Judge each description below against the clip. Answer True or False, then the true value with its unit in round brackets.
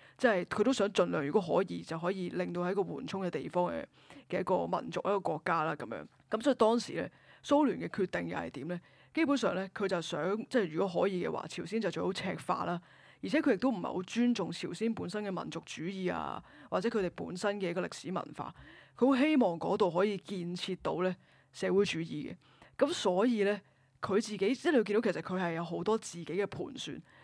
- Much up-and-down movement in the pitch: False (3.7 semitones)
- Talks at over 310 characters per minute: True (330 characters per minute)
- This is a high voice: True (195 Hz)